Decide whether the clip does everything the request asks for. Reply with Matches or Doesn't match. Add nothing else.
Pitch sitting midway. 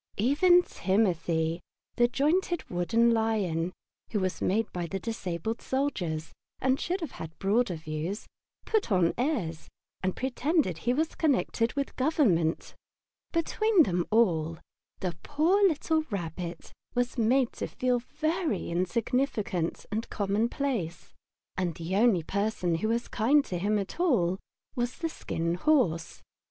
Doesn't match